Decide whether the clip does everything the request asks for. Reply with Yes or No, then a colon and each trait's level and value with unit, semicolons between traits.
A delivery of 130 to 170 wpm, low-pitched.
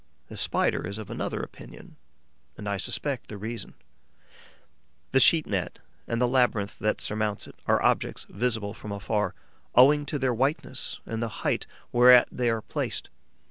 Yes: average, 160 wpm; low, 115 Hz